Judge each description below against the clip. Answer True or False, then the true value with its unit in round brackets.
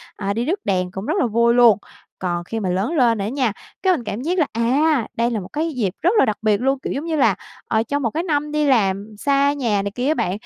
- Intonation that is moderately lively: False (5.8 semitones)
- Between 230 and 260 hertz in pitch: True (235 Hz)